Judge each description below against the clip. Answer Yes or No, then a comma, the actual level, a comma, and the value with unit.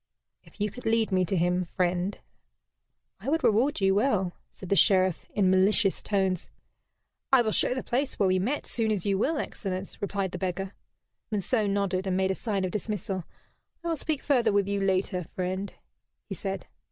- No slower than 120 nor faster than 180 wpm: No, average, 190 wpm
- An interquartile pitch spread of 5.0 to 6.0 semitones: No, average, 2.8 semitones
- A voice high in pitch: Yes, high, 195 Hz